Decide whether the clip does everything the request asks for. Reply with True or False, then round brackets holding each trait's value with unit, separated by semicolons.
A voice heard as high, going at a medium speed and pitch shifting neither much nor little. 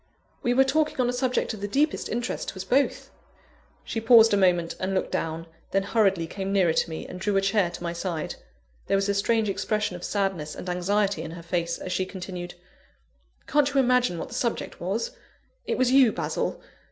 False (195 Hz; 210 wpm; 4.7 semitones)